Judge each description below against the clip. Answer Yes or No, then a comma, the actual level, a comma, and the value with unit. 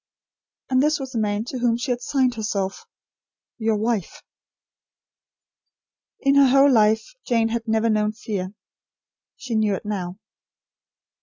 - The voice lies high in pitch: Yes, high, 225 Hz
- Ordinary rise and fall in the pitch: Yes, average, 3.2 semitones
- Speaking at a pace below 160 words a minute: Yes, average, 140 wpm